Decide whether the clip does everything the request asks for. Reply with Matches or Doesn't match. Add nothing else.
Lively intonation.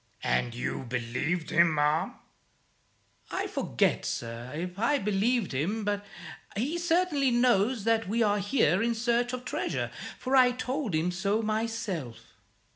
Matches